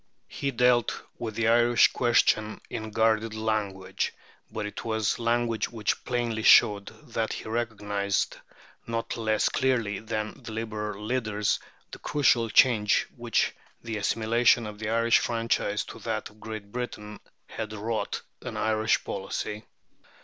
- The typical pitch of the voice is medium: No, low, 110 Hz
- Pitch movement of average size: No, narrow, 1.6 semitones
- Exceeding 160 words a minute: No, slow, 135 wpm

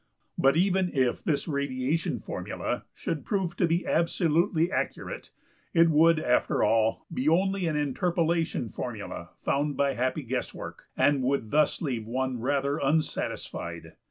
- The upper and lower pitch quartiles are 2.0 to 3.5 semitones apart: No, average, 4.2 semitones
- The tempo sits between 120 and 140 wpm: Yes, slow, 135 wpm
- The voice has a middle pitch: Yes, medium, 150 Hz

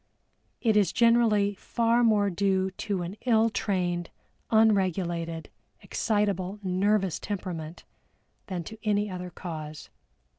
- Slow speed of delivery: Yes, slow, 110 wpm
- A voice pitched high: Yes, high, 195 Hz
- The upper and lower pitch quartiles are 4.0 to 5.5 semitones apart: No, average, 3.1 semitones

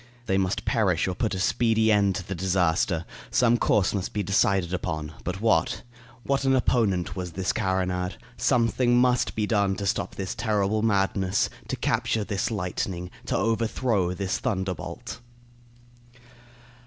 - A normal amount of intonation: Yes, average, 3.3 semitones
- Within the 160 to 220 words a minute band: No, average, 150 wpm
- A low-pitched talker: Yes, low, 100 Hz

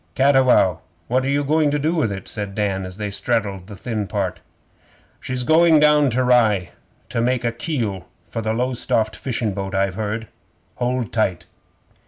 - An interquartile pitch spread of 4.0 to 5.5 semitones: Yes, average, 4.4 semitones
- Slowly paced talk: No, average, 175 wpm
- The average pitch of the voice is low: Yes, low, 115 Hz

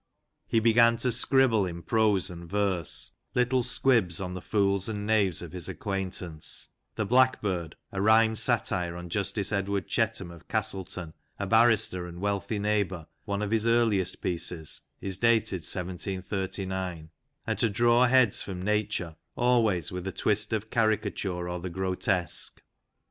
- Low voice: Yes, low, 100 Hz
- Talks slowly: No, average, 150 wpm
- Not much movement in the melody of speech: No, average, 3.6 semitones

